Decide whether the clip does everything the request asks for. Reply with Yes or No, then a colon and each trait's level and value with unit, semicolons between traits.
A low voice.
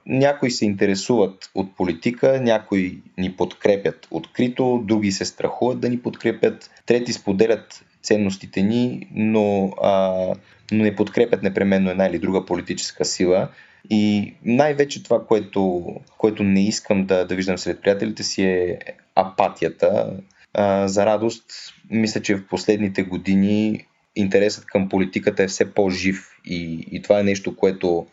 Yes: low, 100 Hz